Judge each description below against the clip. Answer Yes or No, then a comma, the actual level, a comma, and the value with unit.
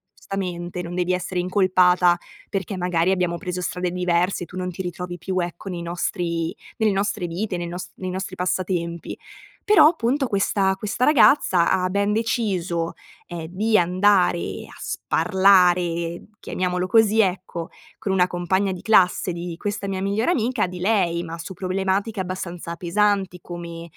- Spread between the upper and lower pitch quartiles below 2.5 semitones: Yes, narrow, 2.1 semitones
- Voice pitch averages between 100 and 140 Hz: No, medium, 185 Hz